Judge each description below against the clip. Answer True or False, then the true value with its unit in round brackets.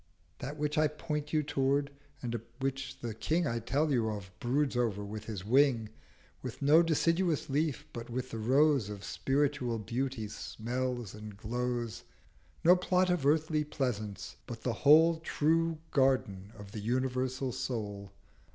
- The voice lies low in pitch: True (130 Hz)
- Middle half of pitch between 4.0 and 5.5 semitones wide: True (4.9 semitones)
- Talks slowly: False (150 wpm)